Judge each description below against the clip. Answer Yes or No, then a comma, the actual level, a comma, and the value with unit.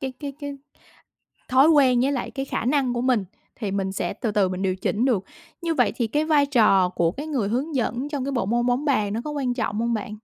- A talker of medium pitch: No, high, 245 Hz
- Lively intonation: No, average, 4.8 semitones